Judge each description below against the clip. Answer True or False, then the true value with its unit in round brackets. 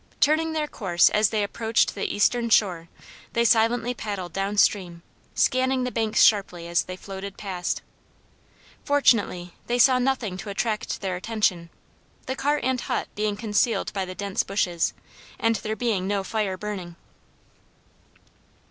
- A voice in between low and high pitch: False (210 Hz)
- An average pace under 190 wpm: True (150 wpm)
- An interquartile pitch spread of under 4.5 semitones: True (3.8 semitones)